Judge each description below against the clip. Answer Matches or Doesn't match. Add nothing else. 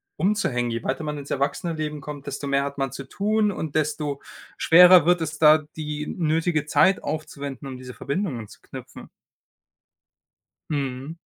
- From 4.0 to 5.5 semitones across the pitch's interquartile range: Doesn't match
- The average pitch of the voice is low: Doesn't match